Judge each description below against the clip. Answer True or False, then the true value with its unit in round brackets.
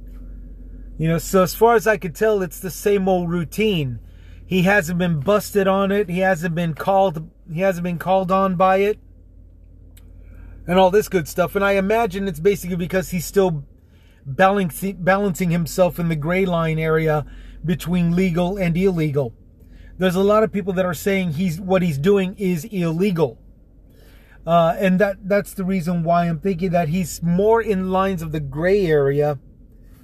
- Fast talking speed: False (175 wpm)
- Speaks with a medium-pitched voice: True (180 Hz)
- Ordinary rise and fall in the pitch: True (3.5 semitones)